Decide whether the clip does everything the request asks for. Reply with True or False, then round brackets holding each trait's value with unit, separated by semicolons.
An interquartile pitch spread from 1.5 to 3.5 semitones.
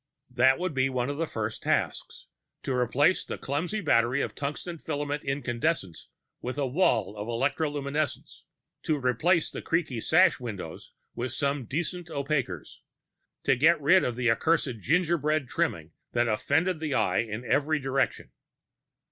False (4.2 semitones)